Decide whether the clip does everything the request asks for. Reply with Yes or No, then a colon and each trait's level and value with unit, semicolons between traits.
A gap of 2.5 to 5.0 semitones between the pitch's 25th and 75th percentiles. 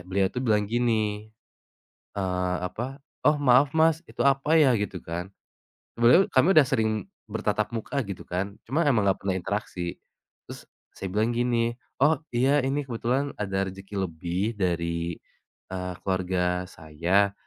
No: wide, 5.4 semitones